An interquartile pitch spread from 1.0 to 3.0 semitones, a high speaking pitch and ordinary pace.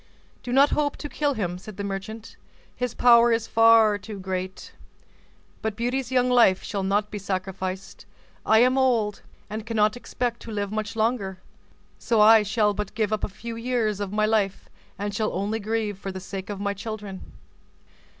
Yes: narrow, 2.5 semitones; high, 215 Hz; average, 180 wpm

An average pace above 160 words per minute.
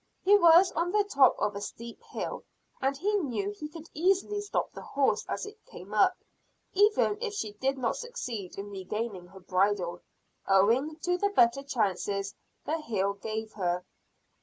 Yes: average, 170 wpm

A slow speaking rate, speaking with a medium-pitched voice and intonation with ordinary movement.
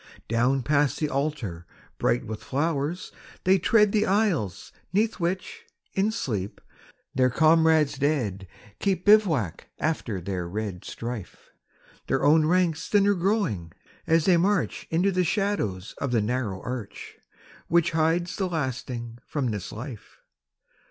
No: slow, 130 wpm; medium, 145 Hz; wide, 8.1 semitones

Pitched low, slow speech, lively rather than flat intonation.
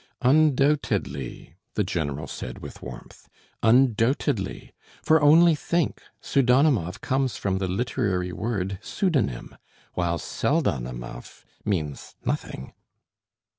Yes: low, 105 Hz; slow, 110 wpm; wide, 8.6 semitones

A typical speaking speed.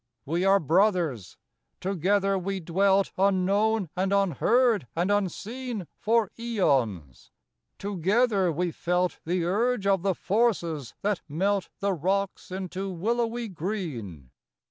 No: slow, 115 wpm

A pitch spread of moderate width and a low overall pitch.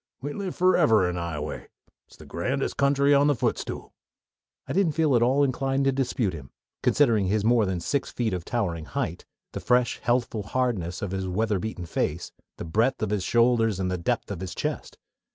No: wide, 6.3 semitones; low, 115 Hz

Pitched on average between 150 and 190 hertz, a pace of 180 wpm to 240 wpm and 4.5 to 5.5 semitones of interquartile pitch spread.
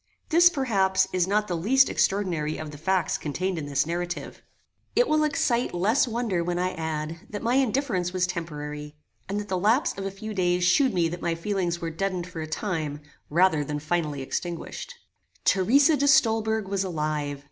Yes: medium, 185 Hz; average, 185 wpm; average, 4.8 semitones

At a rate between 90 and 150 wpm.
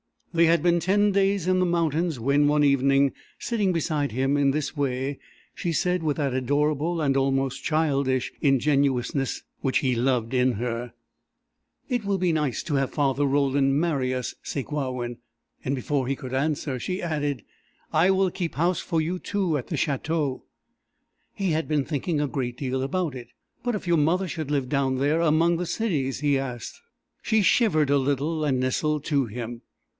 No: average, 180 wpm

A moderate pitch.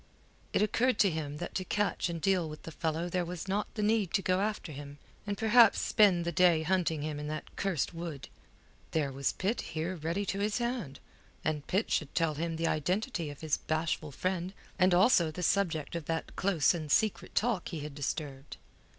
Yes: medium, 170 Hz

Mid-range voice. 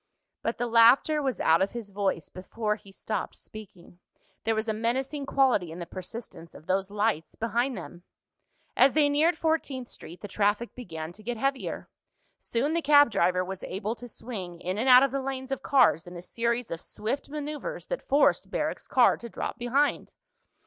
No: high, 230 Hz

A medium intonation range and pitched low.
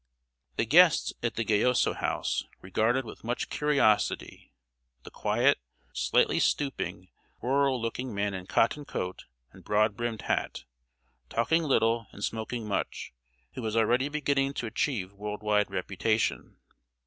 Yes: average, 4.0 semitones; low, 115 Hz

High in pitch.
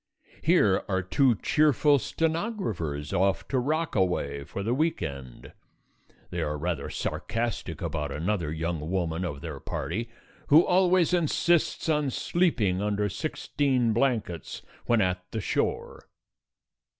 No: low, 105 Hz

